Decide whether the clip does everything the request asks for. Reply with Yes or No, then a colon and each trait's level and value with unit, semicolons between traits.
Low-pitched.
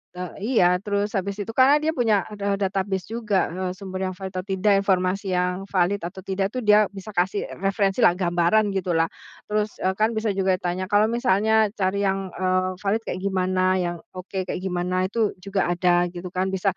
No: high, 190 Hz